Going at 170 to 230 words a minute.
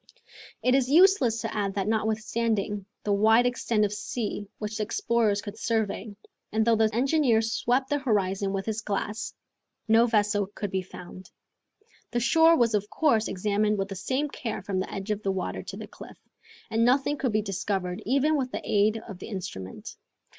Yes: average, 185 wpm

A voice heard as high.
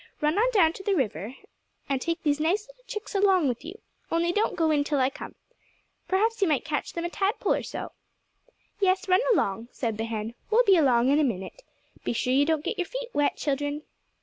Yes: very high, 320 Hz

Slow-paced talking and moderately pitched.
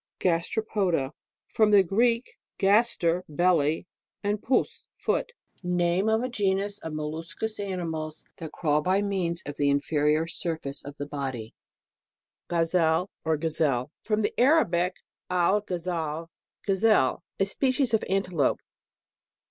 Yes: slow, 130 wpm; medium, 175 Hz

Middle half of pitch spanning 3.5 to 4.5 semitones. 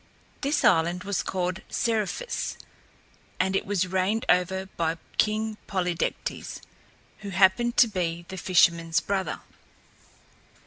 No: average, 3.0 semitones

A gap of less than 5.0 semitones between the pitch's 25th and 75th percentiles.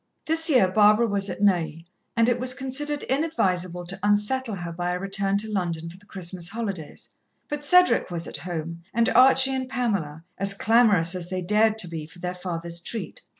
No: average, 5.3 semitones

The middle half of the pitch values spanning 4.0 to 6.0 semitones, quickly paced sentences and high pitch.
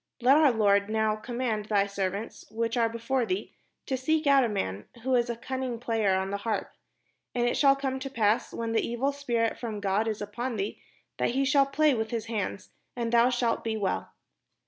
No: average, 3.3 semitones; fast, 215 wpm; high, 230 Hz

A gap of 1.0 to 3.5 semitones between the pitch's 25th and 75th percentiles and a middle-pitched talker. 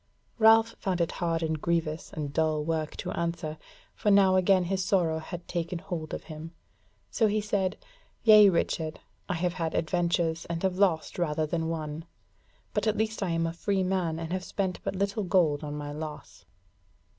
Yes: average, 3.1 semitones; medium, 170 Hz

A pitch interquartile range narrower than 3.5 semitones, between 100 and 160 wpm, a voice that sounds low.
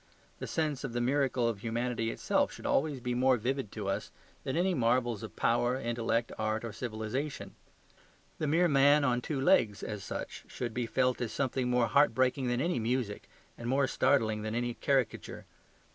No: average, 2.9 semitones; average, 180 wpm; low, 125 Hz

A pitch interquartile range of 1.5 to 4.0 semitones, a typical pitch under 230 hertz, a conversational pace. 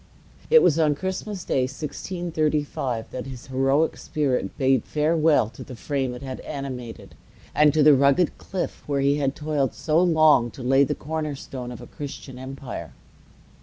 Yes: average, 2.9 semitones; medium, 140 Hz; average, 165 wpm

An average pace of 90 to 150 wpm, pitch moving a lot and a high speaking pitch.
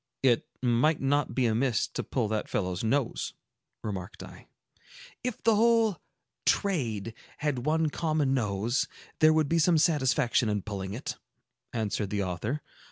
No: average, 145 wpm; wide, 6.4 semitones; low, 130 Hz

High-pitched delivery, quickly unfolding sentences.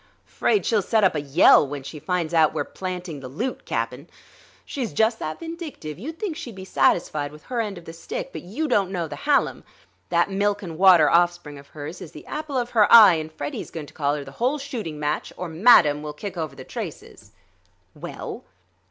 No: medium, 175 Hz; fast, 210 wpm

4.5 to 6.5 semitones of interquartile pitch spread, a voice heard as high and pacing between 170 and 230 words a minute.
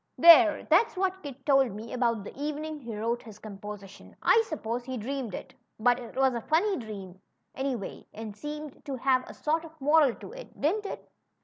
Yes: wide, 5.5 semitones; very high, 265 Hz; average, 200 wpm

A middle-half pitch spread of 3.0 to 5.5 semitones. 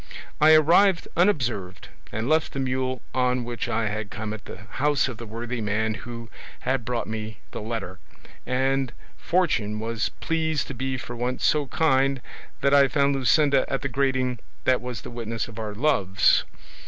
Yes: average, 3.7 semitones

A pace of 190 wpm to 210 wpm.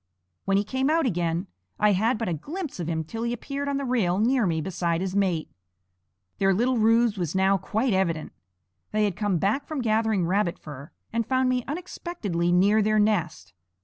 Yes: average, 195 wpm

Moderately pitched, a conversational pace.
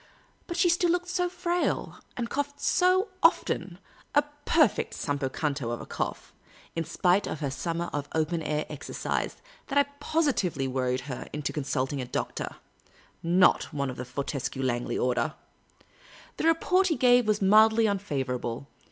Yes: medium, 170 Hz; average, 165 wpm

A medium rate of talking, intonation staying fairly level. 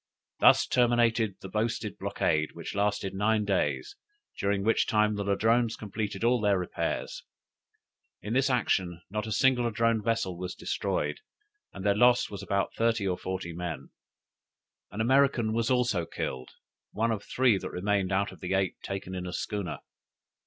No: average, 160 wpm; average, 3.4 semitones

